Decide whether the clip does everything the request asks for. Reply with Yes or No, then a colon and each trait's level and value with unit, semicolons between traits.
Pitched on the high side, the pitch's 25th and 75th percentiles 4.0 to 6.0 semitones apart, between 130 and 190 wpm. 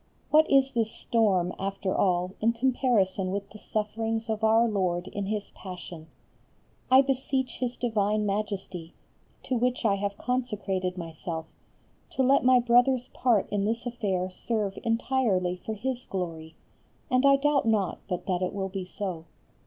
Yes: high, 210 Hz; average, 4.6 semitones; average, 155 wpm